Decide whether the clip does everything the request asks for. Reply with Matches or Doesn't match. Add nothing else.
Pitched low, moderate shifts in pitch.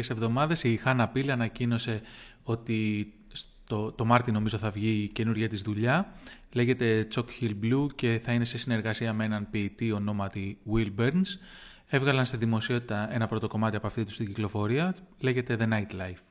Doesn't match